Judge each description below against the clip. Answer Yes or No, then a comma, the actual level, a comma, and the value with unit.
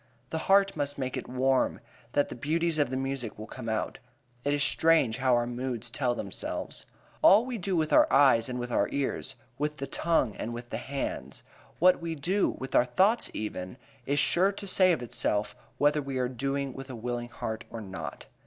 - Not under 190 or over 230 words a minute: Yes, fast, 205 wpm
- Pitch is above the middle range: No, low, 135 Hz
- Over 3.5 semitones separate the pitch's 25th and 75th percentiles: Yes, average, 4.5 semitones